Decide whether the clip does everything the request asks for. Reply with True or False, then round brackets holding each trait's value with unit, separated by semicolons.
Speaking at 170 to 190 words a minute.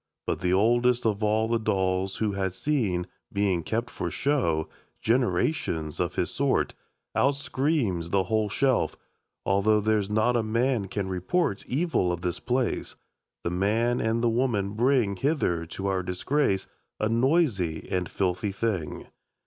False (150 wpm)